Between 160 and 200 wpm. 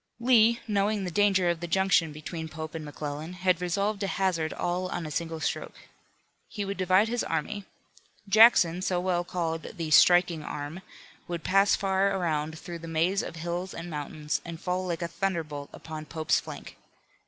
Yes: average, 175 wpm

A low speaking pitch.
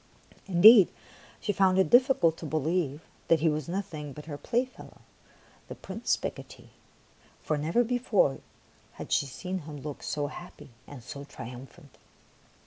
No: medium, 160 Hz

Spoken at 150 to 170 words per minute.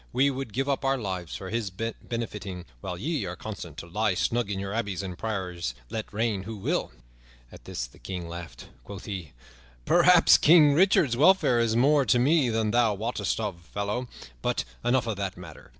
No: average, 190 wpm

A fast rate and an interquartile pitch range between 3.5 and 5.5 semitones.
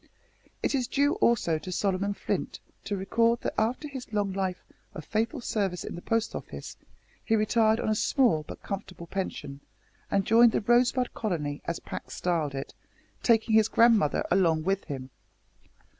No: average, 165 wpm; average, 4.5 semitones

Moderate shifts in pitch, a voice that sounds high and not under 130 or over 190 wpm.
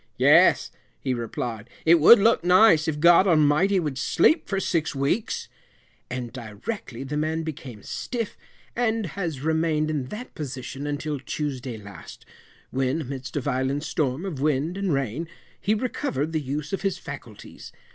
No: average, 4.9 semitones; medium, 150 Hz; average, 155 wpm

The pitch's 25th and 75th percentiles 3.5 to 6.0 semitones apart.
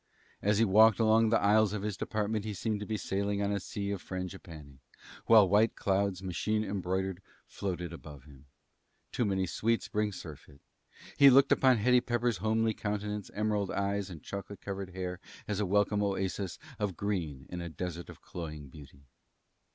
No: average, 2.9 semitones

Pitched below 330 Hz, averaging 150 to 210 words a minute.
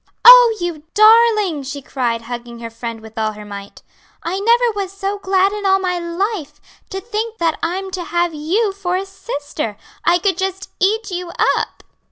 No: very high, 365 Hz; average, 185 wpm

